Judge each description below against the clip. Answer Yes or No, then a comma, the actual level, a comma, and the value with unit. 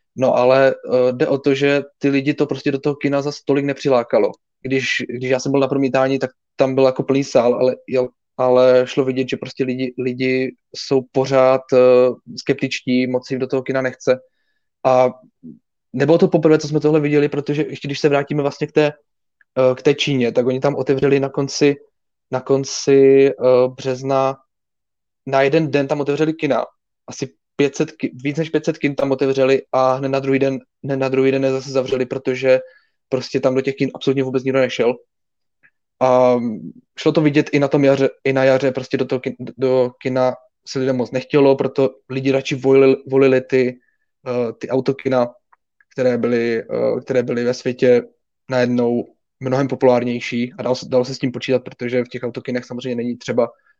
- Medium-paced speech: No, fast, 185 wpm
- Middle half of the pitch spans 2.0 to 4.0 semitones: No, narrow, 1.6 semitones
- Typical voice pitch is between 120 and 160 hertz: Yes, low, 135 Hz